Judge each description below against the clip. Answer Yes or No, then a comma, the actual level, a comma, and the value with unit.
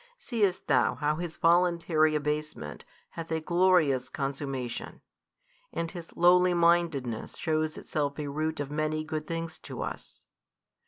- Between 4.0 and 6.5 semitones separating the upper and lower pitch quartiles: No, average, 2.7 semitones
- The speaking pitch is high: No, medium, 155 Hz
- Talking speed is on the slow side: Yes, slow, 130 wpm